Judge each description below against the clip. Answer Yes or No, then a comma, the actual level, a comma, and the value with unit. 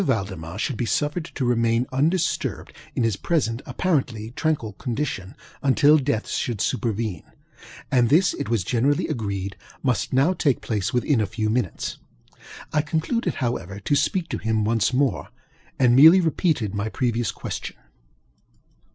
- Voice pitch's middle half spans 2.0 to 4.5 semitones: No, average, 5.2 semitones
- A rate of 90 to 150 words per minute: Yes, average, 140 wpm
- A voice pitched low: Yes, low, 120 Hz